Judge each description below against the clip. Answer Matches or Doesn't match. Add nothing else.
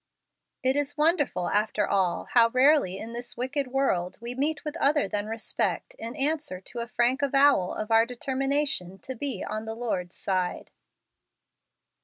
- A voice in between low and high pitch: Doesn't match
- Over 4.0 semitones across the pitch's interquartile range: Matches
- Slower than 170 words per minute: Matches